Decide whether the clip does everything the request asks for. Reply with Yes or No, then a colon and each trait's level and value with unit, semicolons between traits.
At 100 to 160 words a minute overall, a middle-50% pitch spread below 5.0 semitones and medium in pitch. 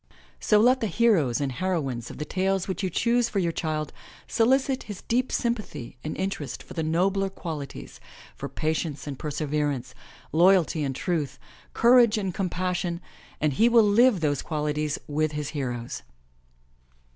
No: average, 155 wpm; wide, 5.6 semitones; medium, 170 Hz